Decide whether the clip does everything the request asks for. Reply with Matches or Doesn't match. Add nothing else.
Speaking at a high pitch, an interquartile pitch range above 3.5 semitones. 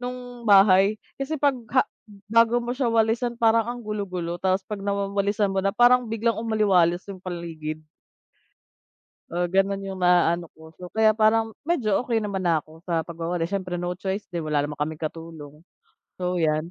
Matches